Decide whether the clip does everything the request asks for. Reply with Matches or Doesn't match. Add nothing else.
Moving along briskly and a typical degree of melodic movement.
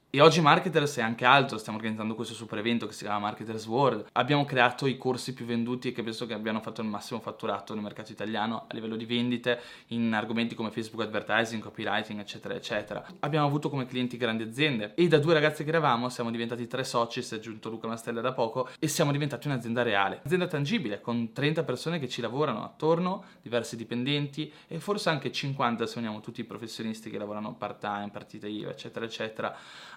Matches